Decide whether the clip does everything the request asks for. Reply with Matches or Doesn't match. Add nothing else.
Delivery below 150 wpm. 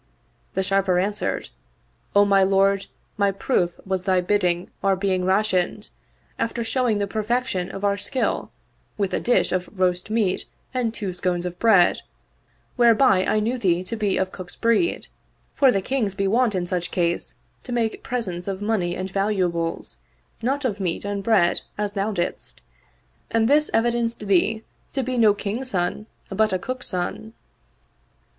Doesn't match